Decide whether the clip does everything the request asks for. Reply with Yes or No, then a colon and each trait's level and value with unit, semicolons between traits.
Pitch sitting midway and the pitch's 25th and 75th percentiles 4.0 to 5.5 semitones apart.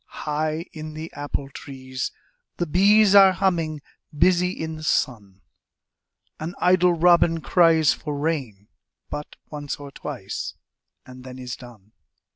Yes: medium, 155 Hz; average, 4.5 semitones